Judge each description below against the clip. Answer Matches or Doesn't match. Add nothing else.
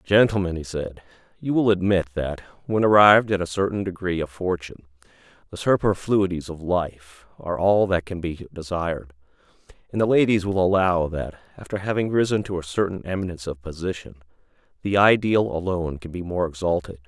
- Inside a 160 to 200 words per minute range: Matches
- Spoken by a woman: Doesn't match